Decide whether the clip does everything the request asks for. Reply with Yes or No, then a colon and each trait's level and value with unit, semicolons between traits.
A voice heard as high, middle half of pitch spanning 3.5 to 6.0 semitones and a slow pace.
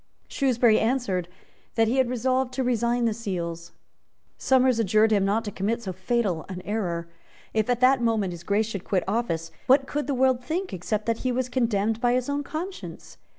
No: high, 230 Hz; average, 4.1 semitones; average, 195 wpm